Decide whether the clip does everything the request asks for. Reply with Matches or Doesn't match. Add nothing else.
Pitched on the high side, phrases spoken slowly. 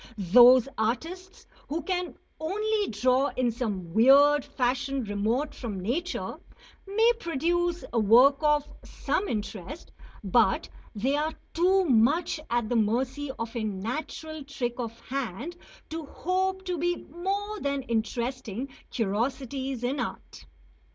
Matches